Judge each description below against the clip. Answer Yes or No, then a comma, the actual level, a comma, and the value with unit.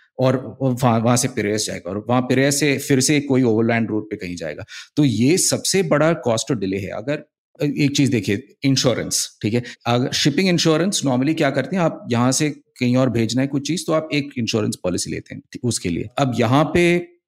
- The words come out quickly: Yes, fast, 210 wpm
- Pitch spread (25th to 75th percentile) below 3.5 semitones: No, average, 3.9 semitones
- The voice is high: No, low, 130 Hz